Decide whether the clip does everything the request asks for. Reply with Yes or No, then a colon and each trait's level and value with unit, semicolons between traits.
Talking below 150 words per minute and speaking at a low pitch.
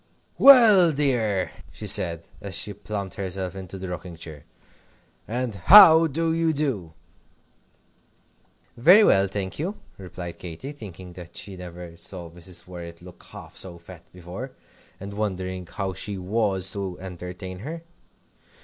Yes: average, 140 wpm; very low, 95 Hz